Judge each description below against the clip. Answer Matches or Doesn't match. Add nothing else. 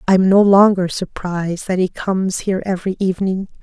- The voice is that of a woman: Matches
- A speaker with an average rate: Matches